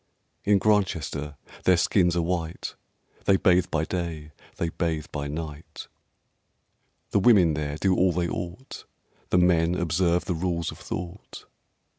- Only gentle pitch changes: Yes, narrow, 2.2 semitones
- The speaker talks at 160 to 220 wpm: No, average, 140 wpm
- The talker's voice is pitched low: Yes, very low, 85 Hz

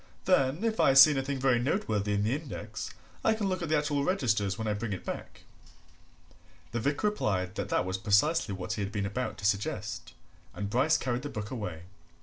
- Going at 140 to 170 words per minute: No, fast, 205 wpm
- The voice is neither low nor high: No, low, 120 Hz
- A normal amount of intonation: No, wide, 6.2 semitones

